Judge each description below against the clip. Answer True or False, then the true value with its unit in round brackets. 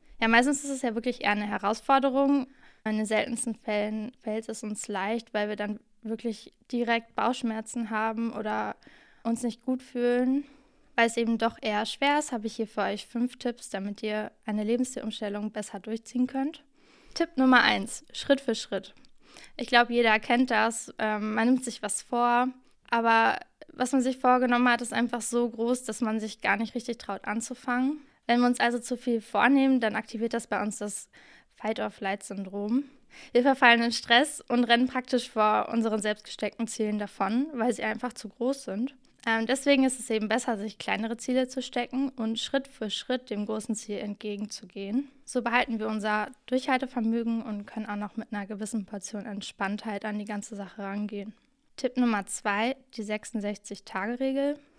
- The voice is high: True (230 Hz)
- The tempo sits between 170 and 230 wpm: True (175 wpm)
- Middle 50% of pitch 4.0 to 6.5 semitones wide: False (2.9 semitones)